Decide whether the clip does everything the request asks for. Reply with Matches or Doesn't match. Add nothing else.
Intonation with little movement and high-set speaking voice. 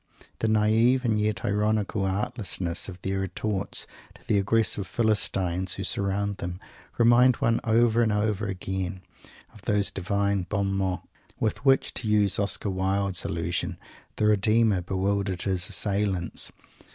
Doesn't match